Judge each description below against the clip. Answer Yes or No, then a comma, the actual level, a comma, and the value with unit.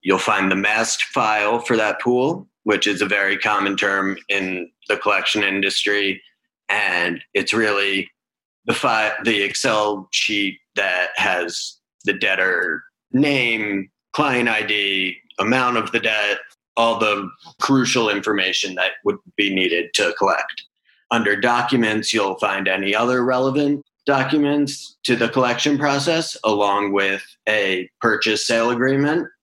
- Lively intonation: No, average, 4.7 semitones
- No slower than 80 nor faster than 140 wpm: Yes, slow, 135 wpm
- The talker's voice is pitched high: No, low, 110 Hz